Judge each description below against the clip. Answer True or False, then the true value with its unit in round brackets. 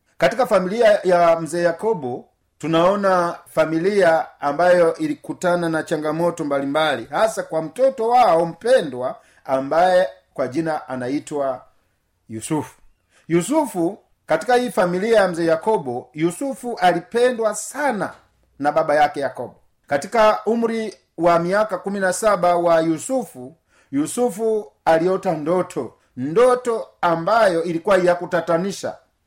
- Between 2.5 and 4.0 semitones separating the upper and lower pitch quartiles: False (5.2 semitones)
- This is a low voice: False (175 Hz)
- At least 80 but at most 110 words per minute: True (105 wpm)